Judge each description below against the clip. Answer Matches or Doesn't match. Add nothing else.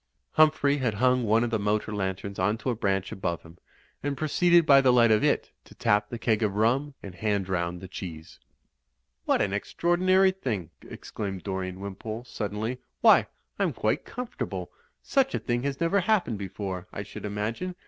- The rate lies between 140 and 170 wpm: Doesn't match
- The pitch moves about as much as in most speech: Doesn't match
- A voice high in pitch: Doesn't match